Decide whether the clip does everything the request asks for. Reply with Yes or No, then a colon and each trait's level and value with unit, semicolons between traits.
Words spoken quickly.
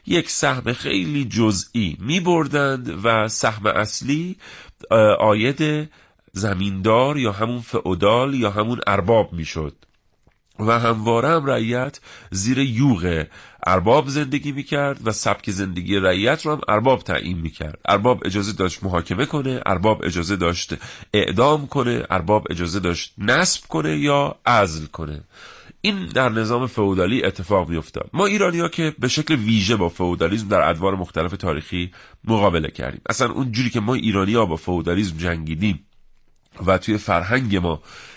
No: average, 145 wpm